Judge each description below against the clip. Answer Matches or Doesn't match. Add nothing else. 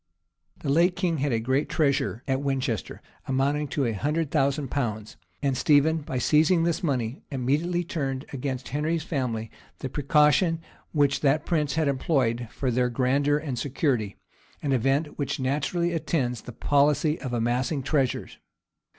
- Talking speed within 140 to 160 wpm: Matches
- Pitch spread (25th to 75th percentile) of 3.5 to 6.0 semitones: Doesn't match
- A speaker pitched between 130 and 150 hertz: Matches